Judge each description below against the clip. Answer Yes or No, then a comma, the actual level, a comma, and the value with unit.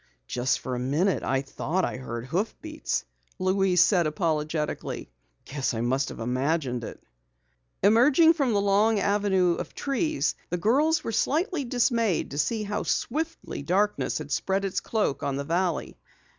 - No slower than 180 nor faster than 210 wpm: No, average, 155 wpm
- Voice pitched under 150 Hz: No, medium, 185 Hz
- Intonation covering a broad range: Yes, wide, 7.9 semitones